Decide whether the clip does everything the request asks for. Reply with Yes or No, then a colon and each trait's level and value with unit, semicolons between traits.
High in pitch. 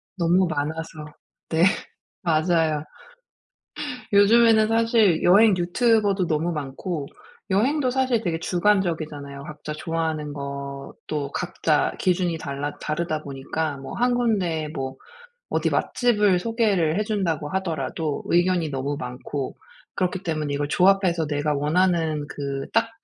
No: medium, 165 Hz